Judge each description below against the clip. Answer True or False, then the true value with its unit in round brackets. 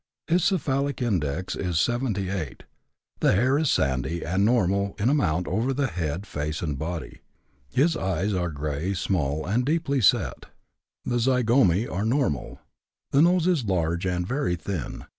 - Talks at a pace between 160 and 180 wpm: False (145 wpm)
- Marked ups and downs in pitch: True (7.5 semitones)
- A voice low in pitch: True (100 Hz)